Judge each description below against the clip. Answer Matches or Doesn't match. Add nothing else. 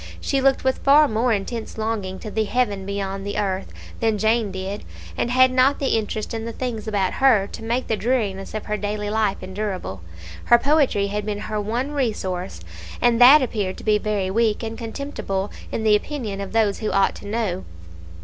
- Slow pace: Doesn't match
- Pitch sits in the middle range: Doesn't match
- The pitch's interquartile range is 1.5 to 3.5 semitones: Matches